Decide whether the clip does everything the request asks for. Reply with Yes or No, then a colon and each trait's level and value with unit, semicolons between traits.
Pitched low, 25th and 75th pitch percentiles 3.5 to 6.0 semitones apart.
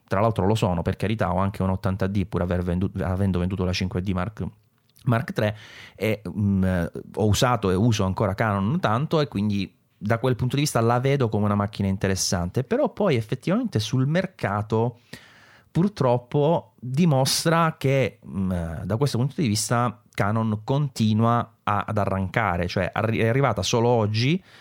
Yes: low, 110 Hz; average, 4.5 semitones